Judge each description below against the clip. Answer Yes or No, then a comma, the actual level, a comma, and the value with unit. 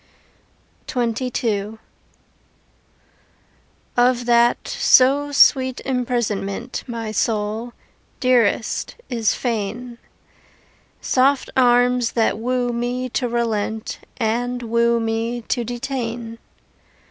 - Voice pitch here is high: Yes, high, 240 Hz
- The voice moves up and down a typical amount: No, narrow, 1.6 semitones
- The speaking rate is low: Yes, slow, 80 wpm